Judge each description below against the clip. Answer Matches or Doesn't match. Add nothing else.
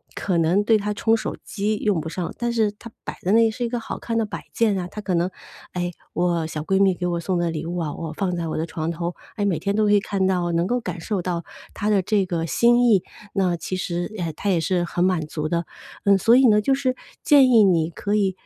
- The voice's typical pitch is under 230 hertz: Matches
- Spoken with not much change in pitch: Doesn't match